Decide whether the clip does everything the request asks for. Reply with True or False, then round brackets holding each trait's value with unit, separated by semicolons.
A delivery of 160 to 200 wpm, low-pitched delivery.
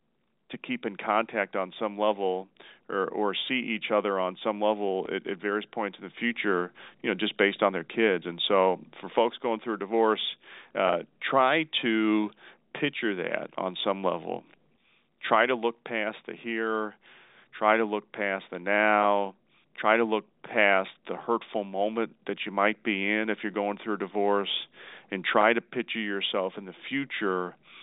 True (180 wpm; 105 Hz)